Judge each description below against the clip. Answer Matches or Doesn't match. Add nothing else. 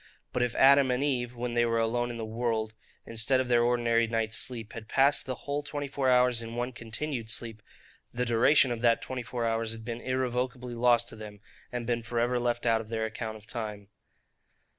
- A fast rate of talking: Matches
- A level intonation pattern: Matches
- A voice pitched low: Matches